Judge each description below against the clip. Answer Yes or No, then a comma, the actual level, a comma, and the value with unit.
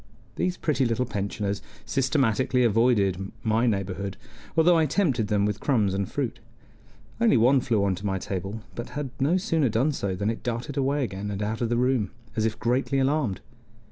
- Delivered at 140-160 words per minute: No, average, 180 wpm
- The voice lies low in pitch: Yes, low, 115 Hz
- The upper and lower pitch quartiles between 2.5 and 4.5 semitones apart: No, average, 4.9 semitones